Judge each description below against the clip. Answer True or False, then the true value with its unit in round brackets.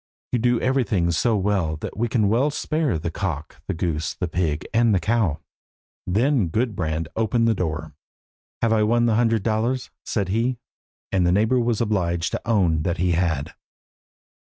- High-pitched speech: False (105 Hz)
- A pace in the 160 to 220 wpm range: True (175 wpm)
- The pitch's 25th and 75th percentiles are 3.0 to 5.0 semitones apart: False (5.4 semitones)